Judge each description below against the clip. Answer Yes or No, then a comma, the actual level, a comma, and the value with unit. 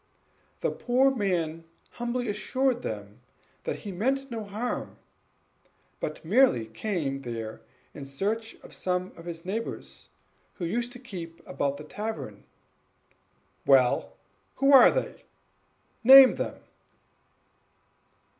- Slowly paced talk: Yes, slow, 115 wpm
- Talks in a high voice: Yes, high, 200 Hz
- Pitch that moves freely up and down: Yes, wide, 8.0 semitones